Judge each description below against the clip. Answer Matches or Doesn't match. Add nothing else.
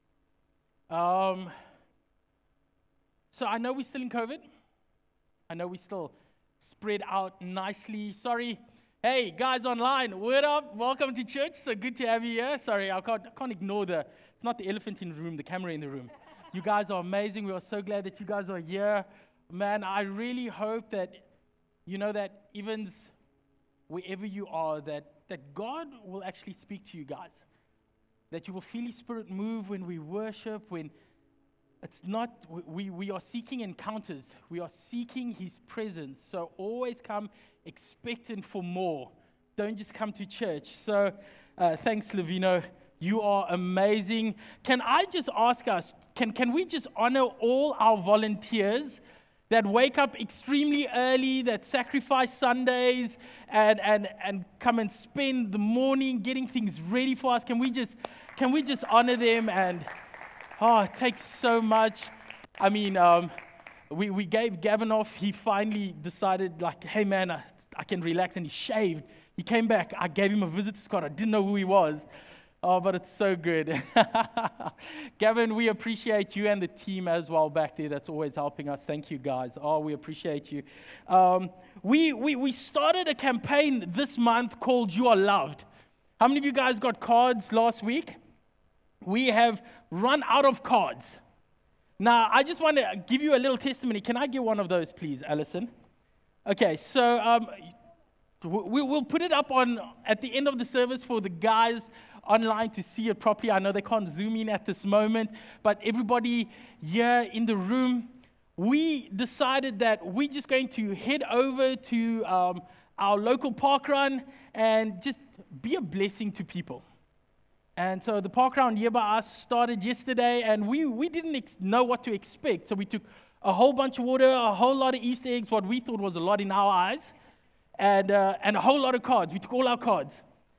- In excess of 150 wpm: Matches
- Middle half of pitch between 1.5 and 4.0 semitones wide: Doesn't match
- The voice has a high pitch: Matches